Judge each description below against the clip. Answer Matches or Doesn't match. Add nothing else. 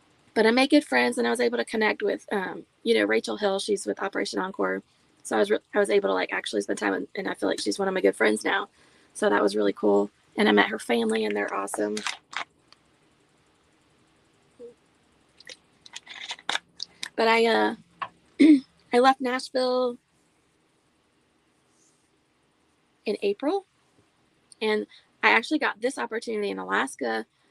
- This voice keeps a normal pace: Matches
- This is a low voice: Doesn't match